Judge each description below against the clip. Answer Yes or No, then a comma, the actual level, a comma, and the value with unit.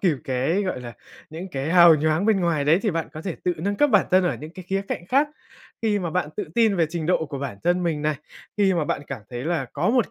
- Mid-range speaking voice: Yes, medium, 170 Hz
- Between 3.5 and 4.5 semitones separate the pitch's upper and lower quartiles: Yes, average, 4.0 semitones